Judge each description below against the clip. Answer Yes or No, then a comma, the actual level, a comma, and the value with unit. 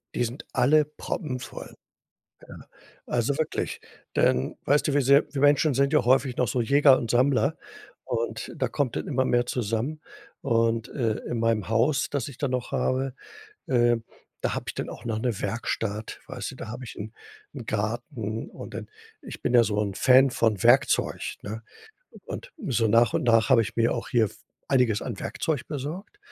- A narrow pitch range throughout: No, average, 3.5 semitones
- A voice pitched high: No, low, 120 Hz